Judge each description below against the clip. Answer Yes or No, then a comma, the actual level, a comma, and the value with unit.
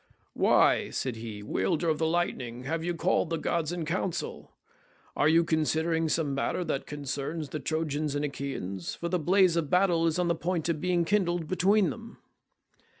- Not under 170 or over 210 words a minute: Yes, average, 175 wpm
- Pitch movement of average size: Yes, average, 3.0 semitones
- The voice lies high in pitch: No, medium, 160 Hz